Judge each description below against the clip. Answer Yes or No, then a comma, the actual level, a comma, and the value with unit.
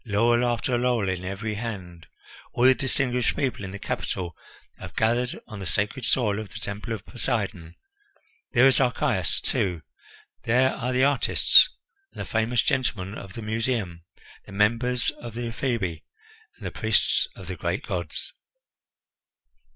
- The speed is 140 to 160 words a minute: Yes, average, 155 wpm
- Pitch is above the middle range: No, low, 115 Hz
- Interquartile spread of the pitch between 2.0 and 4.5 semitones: Yes, average, 3.8 semitones